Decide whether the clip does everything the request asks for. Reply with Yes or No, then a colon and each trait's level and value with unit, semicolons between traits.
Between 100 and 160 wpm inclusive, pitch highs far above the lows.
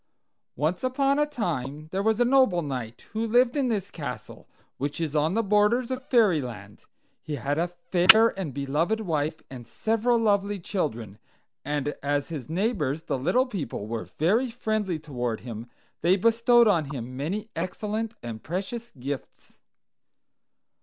Yes: average, 155 wpm; wide, 7.7 semitones